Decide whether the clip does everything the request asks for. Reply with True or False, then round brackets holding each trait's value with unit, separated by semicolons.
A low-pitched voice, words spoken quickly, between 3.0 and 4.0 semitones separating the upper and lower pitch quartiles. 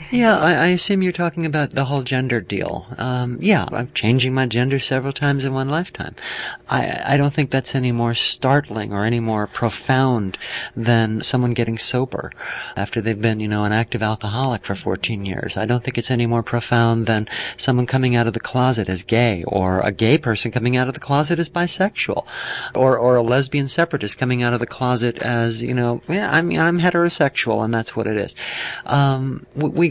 True (125 Hz; 215 wpm; 3.4 semitones)